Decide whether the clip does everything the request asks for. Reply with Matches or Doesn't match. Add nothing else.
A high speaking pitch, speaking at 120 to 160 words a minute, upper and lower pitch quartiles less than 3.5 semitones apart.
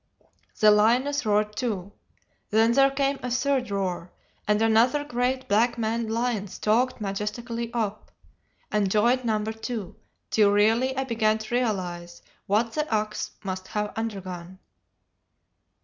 Matches